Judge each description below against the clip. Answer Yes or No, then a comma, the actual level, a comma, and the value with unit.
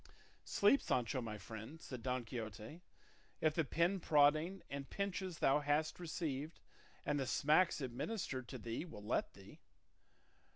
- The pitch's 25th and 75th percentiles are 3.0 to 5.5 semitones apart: Yes, average, 5.1 semitones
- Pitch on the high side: No, medium, 145 Hz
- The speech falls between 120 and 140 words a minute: Yes, slow, 135 wpm